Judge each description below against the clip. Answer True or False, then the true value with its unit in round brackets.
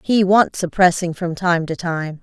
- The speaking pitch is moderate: True (175 Hz)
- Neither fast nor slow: True (190 wpm)